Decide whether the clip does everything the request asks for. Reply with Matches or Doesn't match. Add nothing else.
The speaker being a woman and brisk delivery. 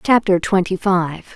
Doesn't match